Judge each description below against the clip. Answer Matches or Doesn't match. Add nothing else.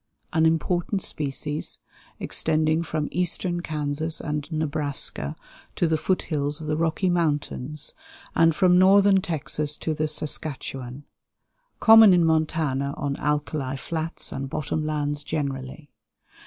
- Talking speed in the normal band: Doesn't match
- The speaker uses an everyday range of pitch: Doesn't match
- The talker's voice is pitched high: Doesn't match